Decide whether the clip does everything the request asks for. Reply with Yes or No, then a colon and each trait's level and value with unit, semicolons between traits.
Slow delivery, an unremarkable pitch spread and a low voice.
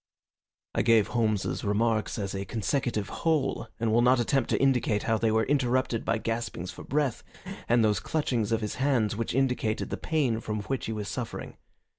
No: average, 185 wpm; average, 3.1 semitones; low, 115 Hz